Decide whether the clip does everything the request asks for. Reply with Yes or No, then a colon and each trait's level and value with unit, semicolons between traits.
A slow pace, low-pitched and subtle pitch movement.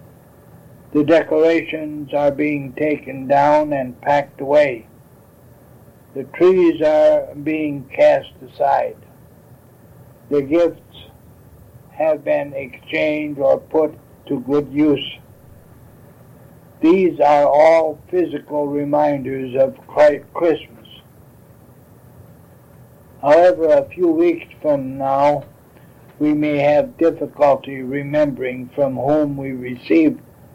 No: slow, 90 wpm; medium, 145 Hz; narrow, 2.3 semitones